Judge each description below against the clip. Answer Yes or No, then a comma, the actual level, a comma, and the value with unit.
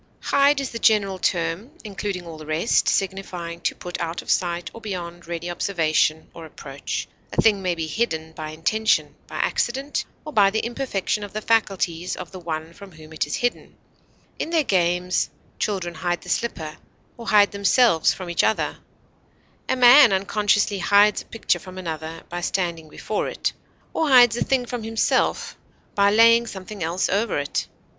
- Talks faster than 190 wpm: No, average, 175 wpm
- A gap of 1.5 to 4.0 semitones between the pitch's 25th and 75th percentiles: No, average, 4.6 semitones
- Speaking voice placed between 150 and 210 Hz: Yes, high, 190 Hz